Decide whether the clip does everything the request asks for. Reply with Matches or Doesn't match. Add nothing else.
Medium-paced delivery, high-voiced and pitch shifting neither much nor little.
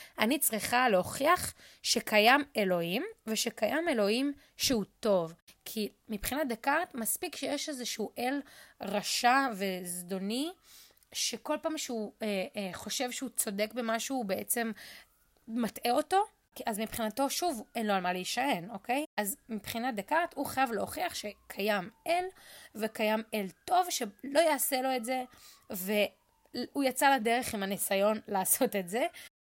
Matches